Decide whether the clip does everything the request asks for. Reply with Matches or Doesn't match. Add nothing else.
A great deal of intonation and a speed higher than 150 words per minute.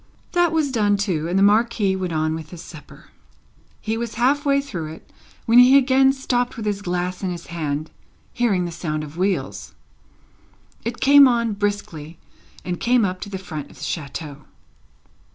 Matches